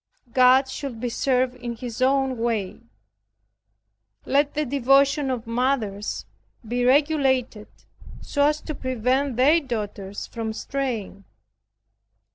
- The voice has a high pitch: Yes, very high, 255 Hz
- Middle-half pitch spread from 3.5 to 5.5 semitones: No, average, 3.1 semitones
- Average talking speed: No, slow, 110 wpm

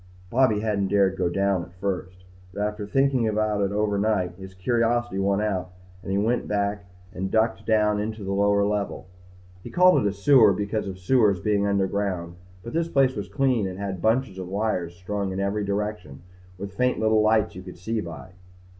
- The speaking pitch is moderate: No, low, 100 Hz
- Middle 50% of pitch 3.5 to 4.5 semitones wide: No, narrow, 2.4 semitones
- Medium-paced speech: Yes, average, 190 wpm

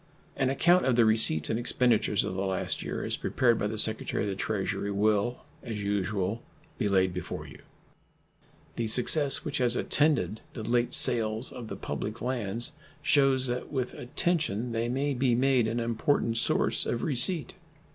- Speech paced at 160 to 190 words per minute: Yes, average, 170 wpm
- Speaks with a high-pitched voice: No, low, 120 Hz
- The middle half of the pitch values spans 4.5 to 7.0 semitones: No, average, 3.5 semitones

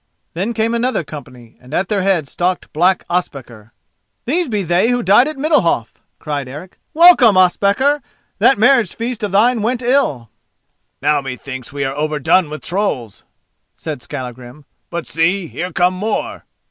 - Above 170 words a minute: No, average, 155 wpm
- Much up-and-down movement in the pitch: Yes, wide, 7.9 semitones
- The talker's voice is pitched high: No, medium, 180 Hz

